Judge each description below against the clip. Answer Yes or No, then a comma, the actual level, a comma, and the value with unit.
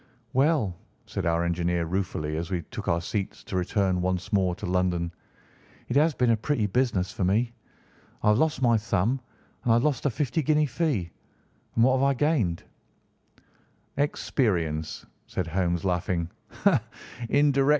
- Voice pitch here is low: Yes, very low, 95 Hz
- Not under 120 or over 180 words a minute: Yes, average, 155 wpm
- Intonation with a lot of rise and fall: Yes, wide, 6.7 semitones